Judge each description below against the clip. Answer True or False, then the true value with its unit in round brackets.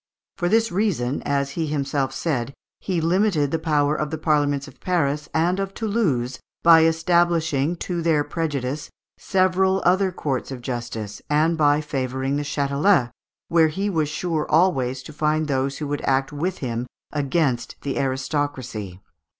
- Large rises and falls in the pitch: False (3.7 semitones)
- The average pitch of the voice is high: False (150 Hz)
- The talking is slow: False (150 wpm)